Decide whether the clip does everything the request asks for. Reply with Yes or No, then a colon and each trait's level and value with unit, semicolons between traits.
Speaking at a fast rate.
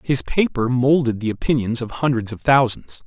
No: average, 175 wpm